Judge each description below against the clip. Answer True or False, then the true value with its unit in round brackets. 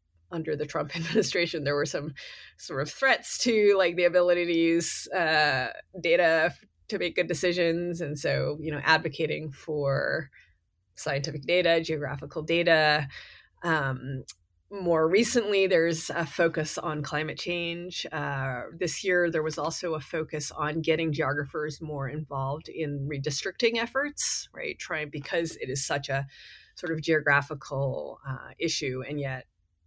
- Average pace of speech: True (145 wpm)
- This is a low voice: False (155 Hz)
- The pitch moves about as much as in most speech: True (3.0 semitones)